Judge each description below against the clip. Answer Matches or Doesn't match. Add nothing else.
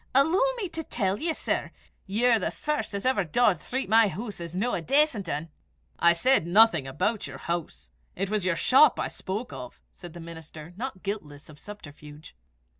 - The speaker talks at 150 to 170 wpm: Doesn't match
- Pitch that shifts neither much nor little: Doesn't match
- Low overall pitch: Doesn't match